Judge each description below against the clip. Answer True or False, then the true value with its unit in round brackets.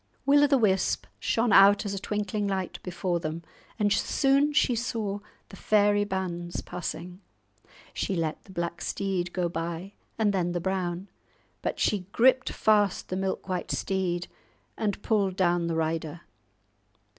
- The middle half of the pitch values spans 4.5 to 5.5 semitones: False (2.9 semitones)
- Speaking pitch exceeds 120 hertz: True (190 Hz)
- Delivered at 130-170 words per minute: True (155 wpm)